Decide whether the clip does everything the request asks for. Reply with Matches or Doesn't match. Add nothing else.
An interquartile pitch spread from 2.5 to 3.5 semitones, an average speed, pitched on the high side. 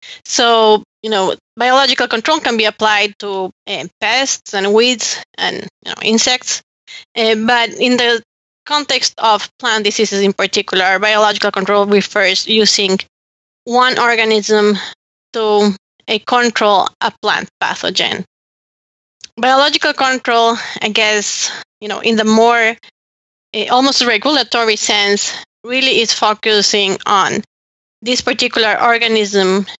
Doesn't match